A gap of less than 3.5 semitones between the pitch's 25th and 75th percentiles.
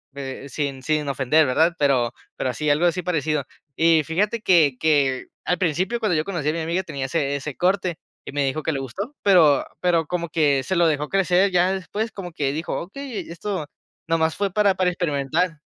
No: average, 4.0 semitones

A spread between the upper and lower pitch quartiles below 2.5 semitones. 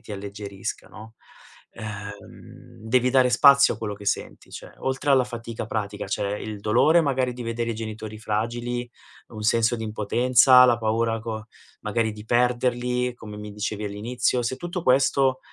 No: average, 2.8 semitones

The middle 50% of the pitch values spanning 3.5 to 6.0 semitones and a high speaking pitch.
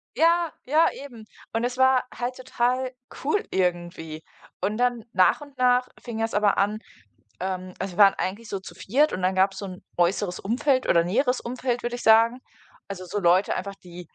Yes: average, 5.2 semitones; high, 220 Hz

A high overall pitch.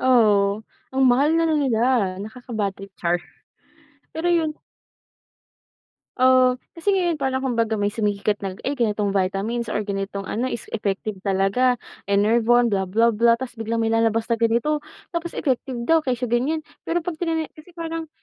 Yes: high, 235 Hz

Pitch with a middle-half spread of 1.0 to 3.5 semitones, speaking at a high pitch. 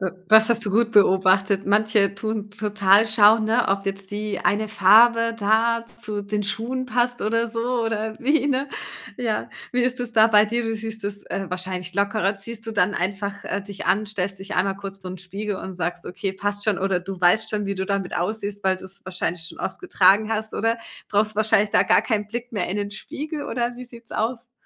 Yes: narrow, 2.4 semitones; high, 210 Hz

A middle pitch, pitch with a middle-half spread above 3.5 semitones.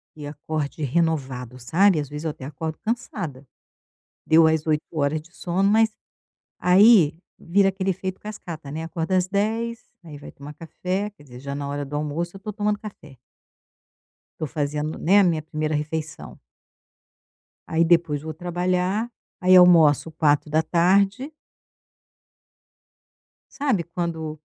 Yes: medium, 165 Hz; average, 4.0 semitones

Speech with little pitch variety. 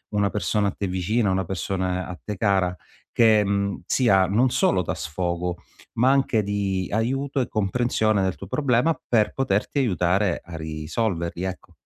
No: average, 3.7 semitones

